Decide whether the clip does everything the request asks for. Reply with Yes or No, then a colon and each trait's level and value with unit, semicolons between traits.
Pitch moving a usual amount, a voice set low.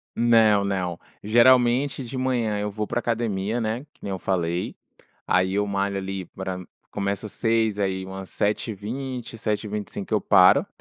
Yes: average, 3.2 semitones; low, 105 Hz